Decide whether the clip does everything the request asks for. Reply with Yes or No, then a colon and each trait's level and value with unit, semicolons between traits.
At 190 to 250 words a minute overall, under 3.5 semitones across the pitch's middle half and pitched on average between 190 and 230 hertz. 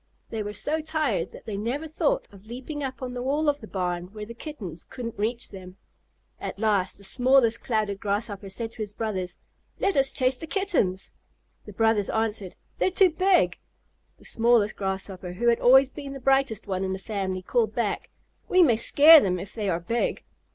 No: average, 200 wpm; wide, 5.6 semitones; high, 225 Hz